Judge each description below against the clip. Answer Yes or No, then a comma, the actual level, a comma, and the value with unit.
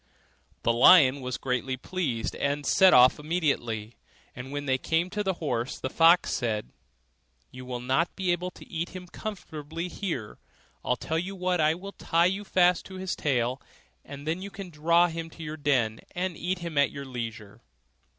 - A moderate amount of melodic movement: No, wide, 5.7 semitones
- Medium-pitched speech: Yes, medium, 155 Hz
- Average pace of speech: Yes, average, 185 wpm